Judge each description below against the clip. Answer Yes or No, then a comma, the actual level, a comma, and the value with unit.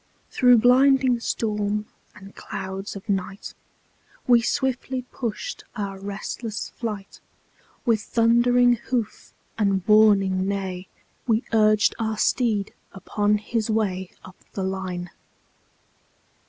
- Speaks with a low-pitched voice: No, high, 210 Hz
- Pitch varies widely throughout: No, average, 3.3 semitones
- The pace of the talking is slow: Yes, slow, 105 wpm